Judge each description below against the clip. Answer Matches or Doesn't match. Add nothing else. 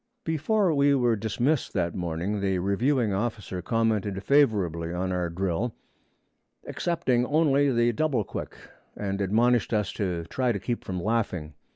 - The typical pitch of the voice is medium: Doesn't match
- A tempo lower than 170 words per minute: Matches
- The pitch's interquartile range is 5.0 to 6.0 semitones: Matches